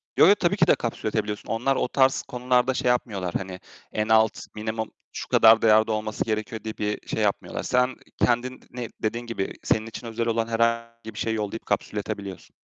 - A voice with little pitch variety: Yes, narrow, 2.0 semitones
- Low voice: Yes, low, 115 Hz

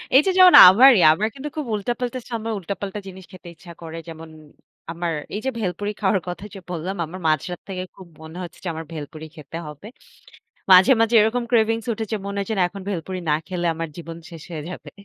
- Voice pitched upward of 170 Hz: Yes, medium, 185 Hz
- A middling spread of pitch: Yes, average, 4.7 semitones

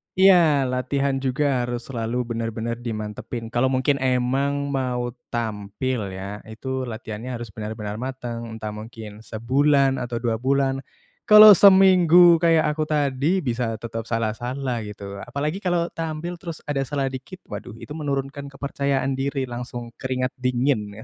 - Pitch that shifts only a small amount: No, average, 3.6 semitones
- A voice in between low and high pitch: No, low, 130 Hz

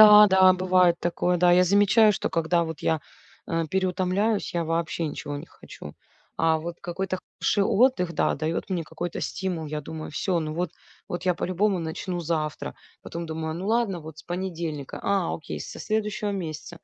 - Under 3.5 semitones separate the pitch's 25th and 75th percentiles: Yes, average, 2.9 semitones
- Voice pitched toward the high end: No, medium, 175 Hz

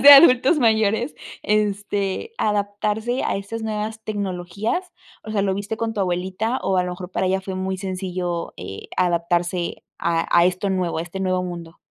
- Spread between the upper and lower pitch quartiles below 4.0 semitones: Yes, average, 3.2 semitones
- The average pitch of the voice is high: Yes, high, 195 Hz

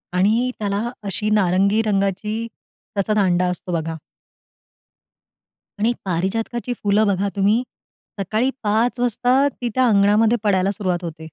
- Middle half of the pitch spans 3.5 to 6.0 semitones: No, average, 2.9 semitones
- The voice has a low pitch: No, high, 205 Hz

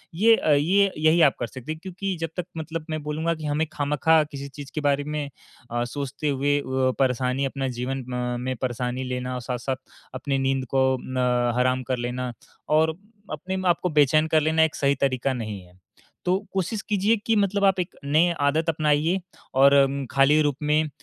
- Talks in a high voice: No, medium, 145 Hz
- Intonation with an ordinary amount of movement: Yes, average, 3.6 semitones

